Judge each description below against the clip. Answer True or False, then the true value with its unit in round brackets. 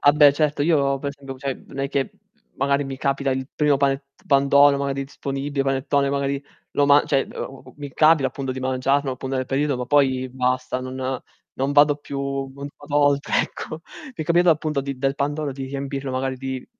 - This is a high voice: False (140 Hz)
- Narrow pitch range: True (1.3 semitones)